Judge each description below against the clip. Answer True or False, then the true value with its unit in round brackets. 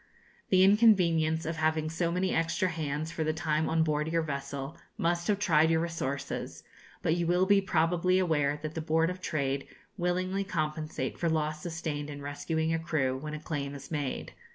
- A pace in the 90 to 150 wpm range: False (185 wpm)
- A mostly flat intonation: True (2.2 semitones)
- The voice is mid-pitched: True (160 Hz)